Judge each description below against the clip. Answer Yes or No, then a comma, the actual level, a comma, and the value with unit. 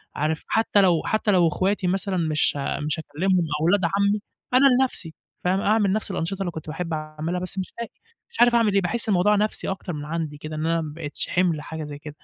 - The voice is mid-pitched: Yes, medium, 180 Hz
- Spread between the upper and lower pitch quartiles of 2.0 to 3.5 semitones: No, average, 4.2 semitones